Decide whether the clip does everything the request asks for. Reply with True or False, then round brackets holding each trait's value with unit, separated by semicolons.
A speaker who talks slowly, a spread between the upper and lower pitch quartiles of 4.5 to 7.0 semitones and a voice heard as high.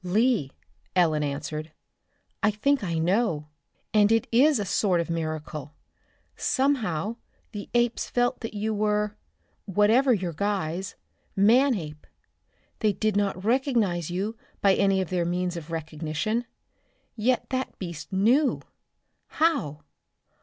True (125 wpm; 5.4 semitones; 200 Hz)